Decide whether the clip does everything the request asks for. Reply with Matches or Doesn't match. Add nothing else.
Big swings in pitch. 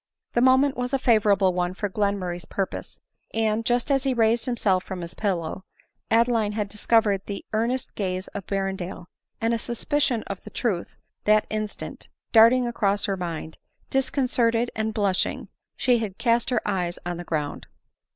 Doesn't match